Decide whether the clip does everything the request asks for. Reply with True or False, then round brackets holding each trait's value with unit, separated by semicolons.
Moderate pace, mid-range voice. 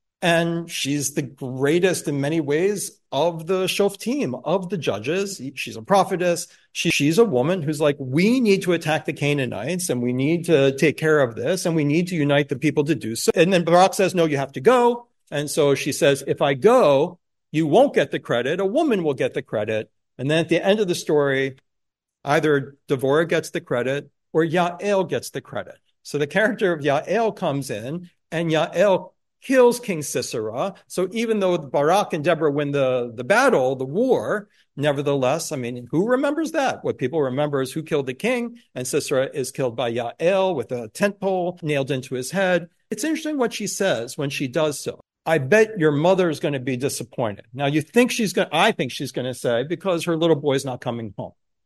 False (210 wpm; 160 Hz)